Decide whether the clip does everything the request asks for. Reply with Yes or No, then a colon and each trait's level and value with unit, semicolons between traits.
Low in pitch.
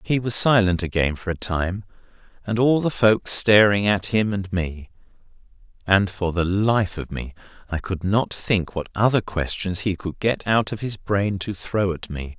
Yes: low, 100 Hz